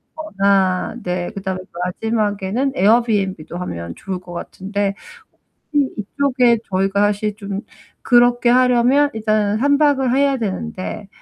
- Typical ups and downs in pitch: Yes, average, 4.2 semitones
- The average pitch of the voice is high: Yes, high, 210 Hz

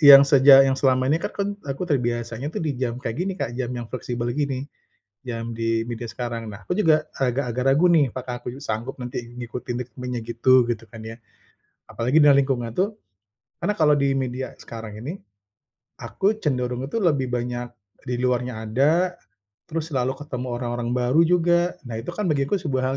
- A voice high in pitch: No, low, 130 Hz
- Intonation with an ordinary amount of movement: Yes, average, 3.3 semitones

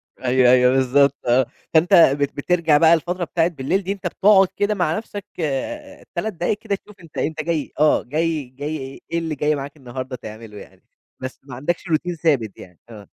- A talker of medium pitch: Yes, medium, 155 Hz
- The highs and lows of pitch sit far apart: No, average, 4.8 semitones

